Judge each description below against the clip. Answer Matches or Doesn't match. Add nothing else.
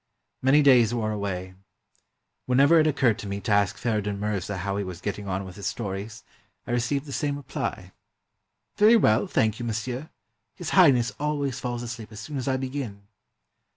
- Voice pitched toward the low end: Matches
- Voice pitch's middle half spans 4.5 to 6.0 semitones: Matches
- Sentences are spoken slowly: Doesn't match